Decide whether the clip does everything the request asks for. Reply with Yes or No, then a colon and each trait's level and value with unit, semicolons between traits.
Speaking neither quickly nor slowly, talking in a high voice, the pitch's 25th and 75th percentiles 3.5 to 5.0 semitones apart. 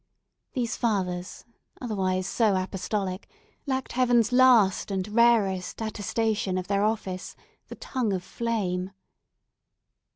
No: slow, 105 wpm; high, 205 Hz; average, 3.8 semitones